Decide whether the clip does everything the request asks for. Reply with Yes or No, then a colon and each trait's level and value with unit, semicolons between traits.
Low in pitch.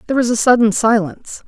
No: high, 225 Hz